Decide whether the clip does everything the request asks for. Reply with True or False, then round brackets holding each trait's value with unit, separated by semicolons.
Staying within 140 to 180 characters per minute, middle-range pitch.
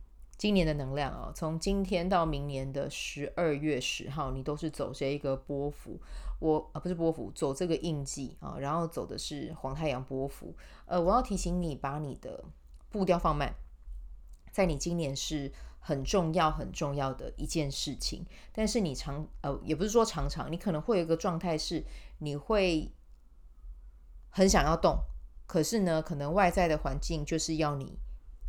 False (255 characters per minute; 150 Hz)